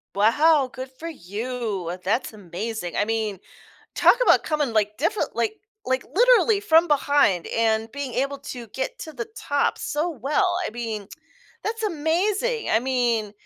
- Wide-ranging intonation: Yes, wide, 6.7 semitones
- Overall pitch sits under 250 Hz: No, very high, 260 Hz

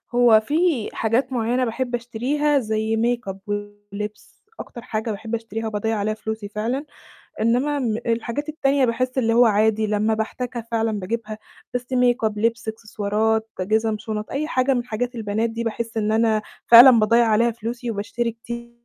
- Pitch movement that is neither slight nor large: No, narrow, 2.0 semitones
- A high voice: Yes, high, 225 Hz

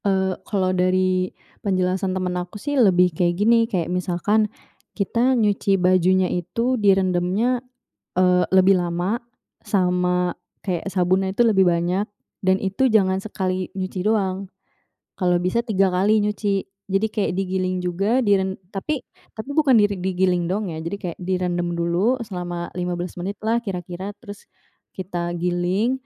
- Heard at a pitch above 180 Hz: Yes, high, 190 Hz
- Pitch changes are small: Yes, narrow, 2.3 semitones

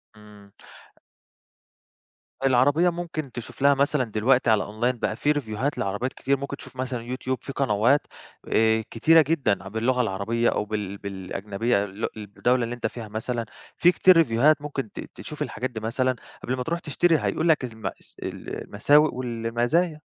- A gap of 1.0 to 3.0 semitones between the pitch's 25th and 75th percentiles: No, average, 4.5 semitones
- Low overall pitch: Yes, low, 125 Hz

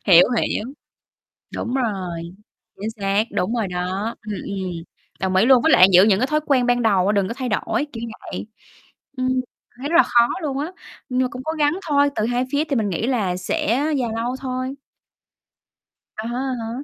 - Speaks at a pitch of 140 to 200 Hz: No, high, 235 Hz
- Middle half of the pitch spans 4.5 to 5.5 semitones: Yes, average, 4.8 semitones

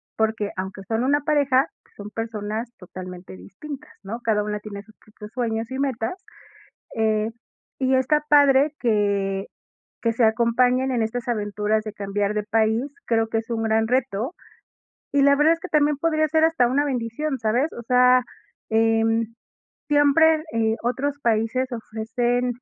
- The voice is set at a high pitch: Yes, high, 230 Hz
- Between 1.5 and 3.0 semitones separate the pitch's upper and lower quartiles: No, average, 3.5 semitones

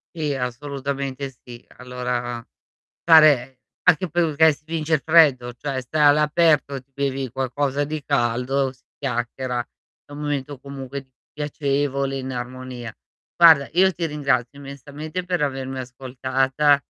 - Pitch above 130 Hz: Yes, medium, 140 Hz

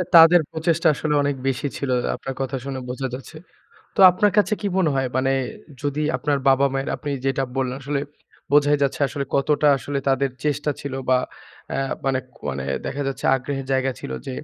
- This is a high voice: No, medium, 140 Hz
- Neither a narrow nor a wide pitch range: No, narrow, 1.8 semitones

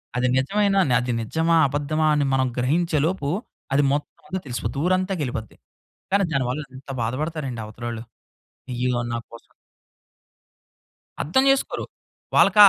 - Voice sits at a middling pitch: Yes, medium, 145 Hz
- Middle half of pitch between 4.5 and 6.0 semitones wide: Yes, average, 5.1 semitones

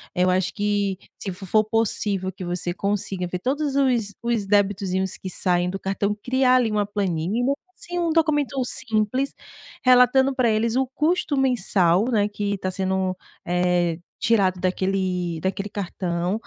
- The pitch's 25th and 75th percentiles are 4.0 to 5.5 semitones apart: Yes, average, 4.8 semitones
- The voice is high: Yes, high, 205 Hz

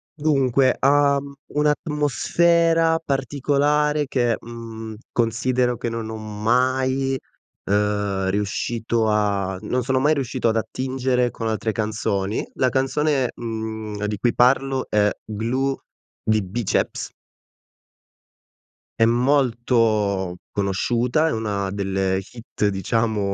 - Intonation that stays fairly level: No, average, 4.1 semitones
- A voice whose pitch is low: Yes, low, 115 Hz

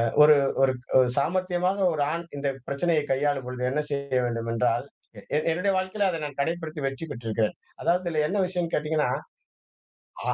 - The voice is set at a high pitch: No, medium, 150 Hz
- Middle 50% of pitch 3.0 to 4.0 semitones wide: No, average, 4.5 semitones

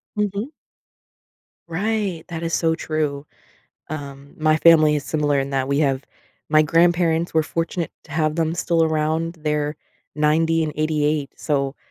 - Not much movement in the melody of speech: Yes, narrow, 1.9 semitones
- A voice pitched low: No, medium, 155 Hz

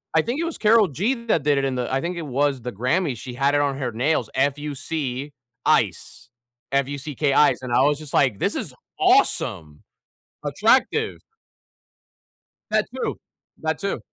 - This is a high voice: No, medium, 140 Hz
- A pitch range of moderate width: Yes, average, 3.7 semitones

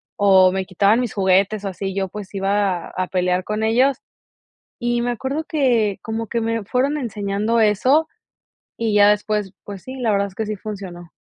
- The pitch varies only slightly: No, average, 3.1 semitones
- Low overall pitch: No, high, 210 Hz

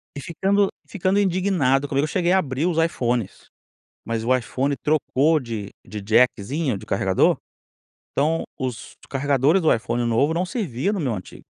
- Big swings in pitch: Yes, wide, 6.0 semitones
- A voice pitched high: No, medium, 140 Hz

